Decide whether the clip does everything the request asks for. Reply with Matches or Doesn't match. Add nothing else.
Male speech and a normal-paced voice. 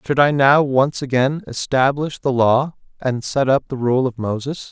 Matches